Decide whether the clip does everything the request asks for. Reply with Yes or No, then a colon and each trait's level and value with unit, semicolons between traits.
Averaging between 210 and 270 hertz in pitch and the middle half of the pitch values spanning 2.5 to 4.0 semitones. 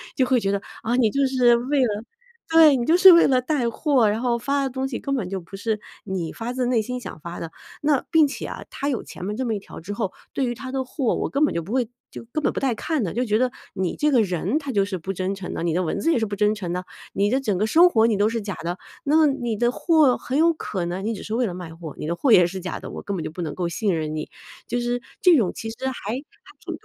No: high, 230 Hz; wide, 5.5 semitones